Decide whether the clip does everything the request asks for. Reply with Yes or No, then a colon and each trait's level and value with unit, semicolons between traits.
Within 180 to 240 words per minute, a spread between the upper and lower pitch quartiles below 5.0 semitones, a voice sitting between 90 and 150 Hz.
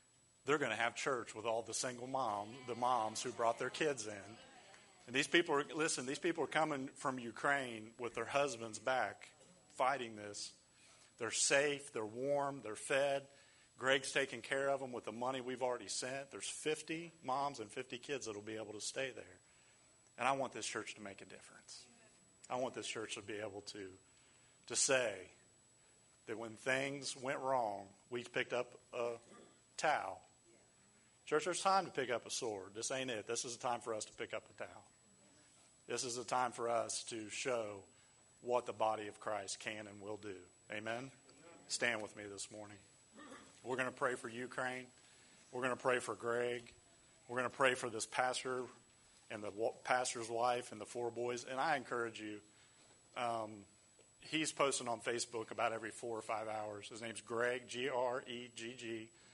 Yes: average, 190 wpm; average, 3.2 semitones; low, 120 Hz